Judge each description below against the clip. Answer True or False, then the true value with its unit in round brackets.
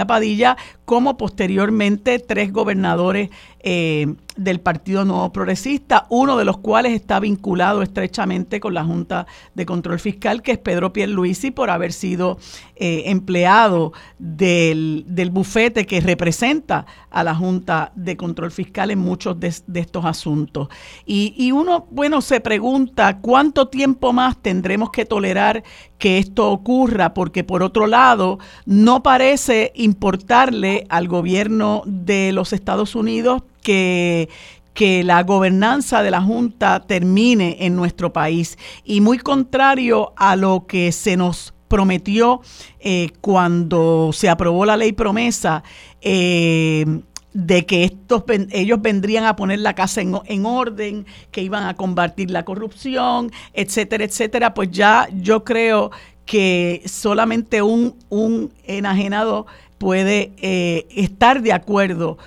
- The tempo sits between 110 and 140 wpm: True (135 wpm)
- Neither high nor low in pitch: False (200 Hz)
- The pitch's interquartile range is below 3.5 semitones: False (3.8 semitones)